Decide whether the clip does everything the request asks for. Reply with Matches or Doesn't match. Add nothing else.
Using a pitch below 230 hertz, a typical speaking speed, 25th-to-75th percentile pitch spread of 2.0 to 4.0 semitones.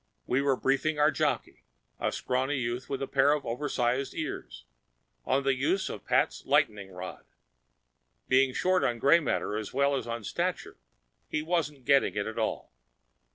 Matches